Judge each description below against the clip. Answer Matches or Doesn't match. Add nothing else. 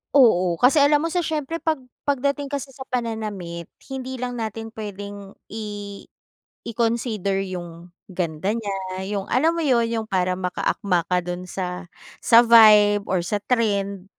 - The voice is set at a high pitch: Matches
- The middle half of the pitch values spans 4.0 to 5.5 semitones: Matches